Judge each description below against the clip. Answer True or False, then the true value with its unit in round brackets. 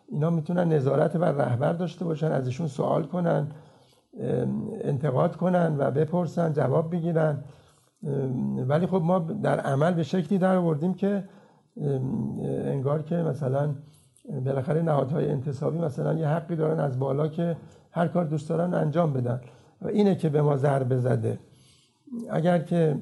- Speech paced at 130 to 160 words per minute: True (140 wpm)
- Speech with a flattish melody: False (3.5 semitones)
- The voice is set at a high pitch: False (155 Hz)